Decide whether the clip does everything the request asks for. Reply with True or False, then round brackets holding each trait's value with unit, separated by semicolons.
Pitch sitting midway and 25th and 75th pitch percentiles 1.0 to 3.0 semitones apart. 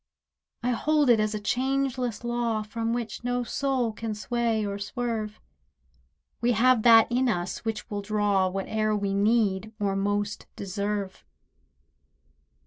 False (220 Hz; 2.7 semitones)